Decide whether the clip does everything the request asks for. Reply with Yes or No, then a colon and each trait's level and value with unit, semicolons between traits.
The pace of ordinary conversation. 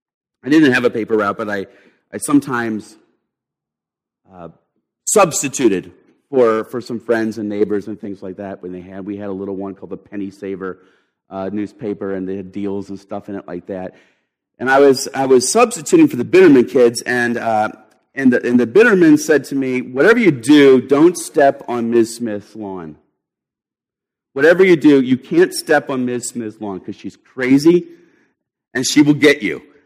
Yes: average, 185 wpm